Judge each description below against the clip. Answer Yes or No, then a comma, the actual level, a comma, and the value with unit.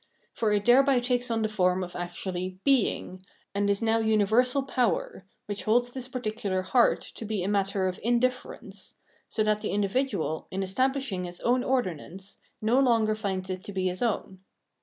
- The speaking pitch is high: Yes, high, 215 Hz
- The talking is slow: No, average, 195 wpm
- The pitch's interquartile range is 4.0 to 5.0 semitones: Yes, average, 4.5 semitones